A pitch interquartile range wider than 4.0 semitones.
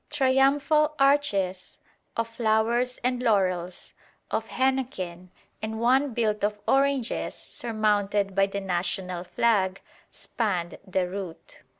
Yes: average, 5.2 semitones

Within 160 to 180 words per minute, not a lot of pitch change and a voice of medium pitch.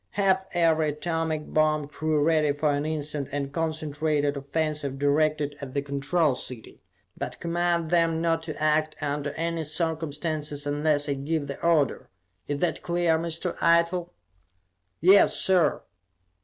No: average, 140 wpm; narrow, 2.3 semitones; medium, 155 Hz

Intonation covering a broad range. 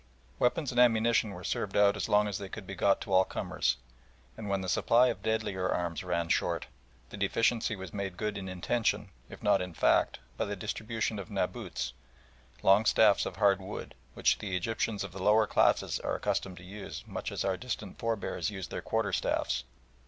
No: average, 2.8 semitones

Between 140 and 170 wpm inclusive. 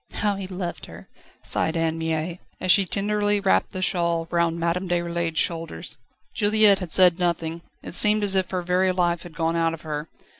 No: average, 190 wpm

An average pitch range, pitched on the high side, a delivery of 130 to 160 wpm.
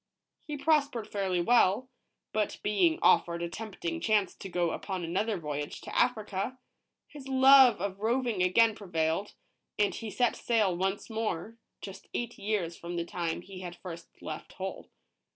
Yes: average, 4.9 semitones; high, 205 Hz; average, 155 wpm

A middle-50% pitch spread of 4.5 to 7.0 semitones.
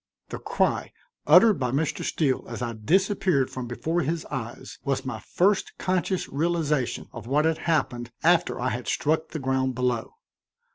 Yes: average, 5.1 semitones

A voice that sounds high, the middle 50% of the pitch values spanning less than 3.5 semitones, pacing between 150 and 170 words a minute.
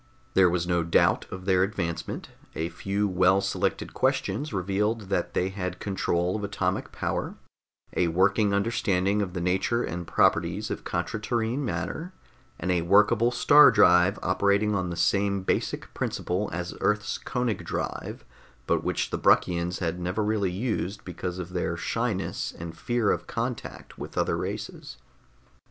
No: very low, 95 Hz; average, 2.8 semitones; average, 155 wpm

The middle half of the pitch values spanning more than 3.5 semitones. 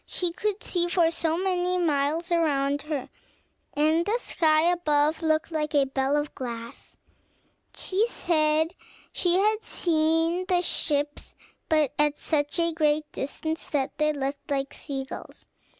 No: average, 2.9 semitones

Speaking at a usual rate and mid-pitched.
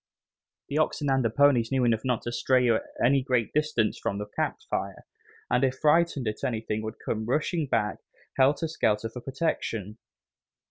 No: average, 165 wpm; low, 125 Hz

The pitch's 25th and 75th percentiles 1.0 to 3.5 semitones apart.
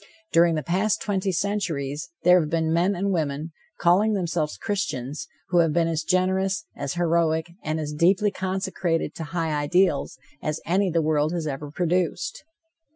Yes: average, 3.1 semitones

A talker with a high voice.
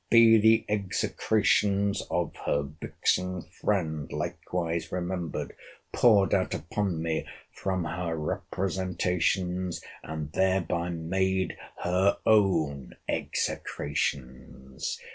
No: very low, 90 Hz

